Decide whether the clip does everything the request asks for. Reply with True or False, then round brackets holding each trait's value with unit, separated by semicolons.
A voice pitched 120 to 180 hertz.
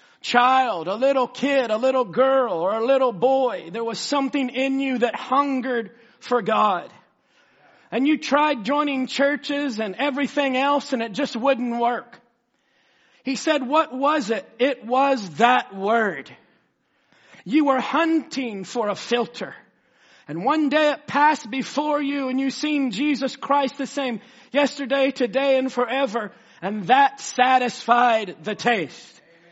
False (260 Hz)